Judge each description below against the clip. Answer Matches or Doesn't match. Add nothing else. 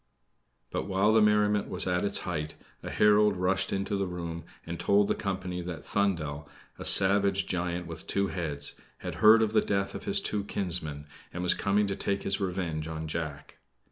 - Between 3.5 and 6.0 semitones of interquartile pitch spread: Doesn't match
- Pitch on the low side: Matches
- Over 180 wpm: Matches